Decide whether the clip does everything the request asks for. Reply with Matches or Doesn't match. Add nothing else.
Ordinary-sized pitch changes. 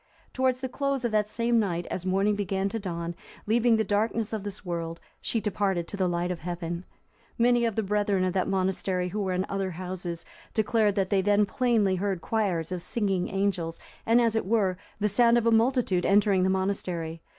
Matches